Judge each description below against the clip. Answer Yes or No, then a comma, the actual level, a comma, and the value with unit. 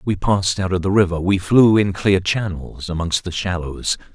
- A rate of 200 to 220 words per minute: Yes, fast, 205 wpm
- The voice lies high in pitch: No, very low, 95 Hz